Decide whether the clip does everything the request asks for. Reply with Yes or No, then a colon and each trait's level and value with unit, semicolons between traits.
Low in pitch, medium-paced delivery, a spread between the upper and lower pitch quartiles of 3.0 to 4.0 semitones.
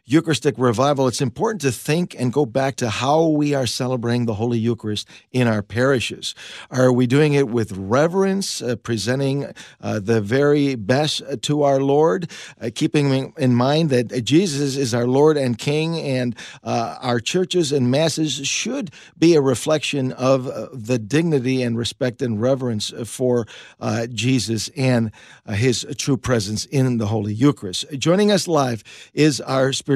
Yes: low, 130 Hz; average, 160 wpm; average, 3.4 semitones